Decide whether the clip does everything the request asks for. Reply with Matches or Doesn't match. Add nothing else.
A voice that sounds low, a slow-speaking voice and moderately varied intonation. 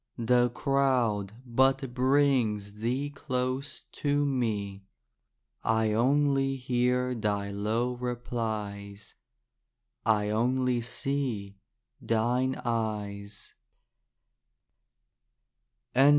Matches